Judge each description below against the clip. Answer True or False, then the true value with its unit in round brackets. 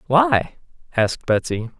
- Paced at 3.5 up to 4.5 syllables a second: True (4.2 syllables/s)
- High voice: False (145 Hz)